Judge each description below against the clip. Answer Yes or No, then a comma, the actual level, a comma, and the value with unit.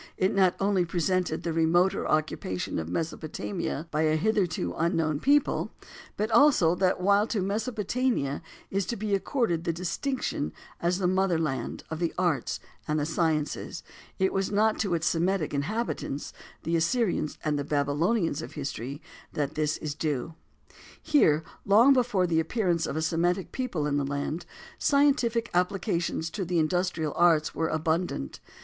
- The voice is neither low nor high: Yes, medium, 175 Hz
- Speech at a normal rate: Yes, average, 150 wpm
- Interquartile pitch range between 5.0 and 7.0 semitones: No, average, 4.3 semitones